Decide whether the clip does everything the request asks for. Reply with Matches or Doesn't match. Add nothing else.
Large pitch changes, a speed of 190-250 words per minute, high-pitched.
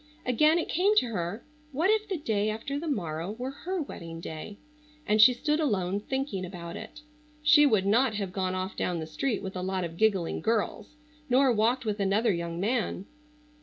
Matches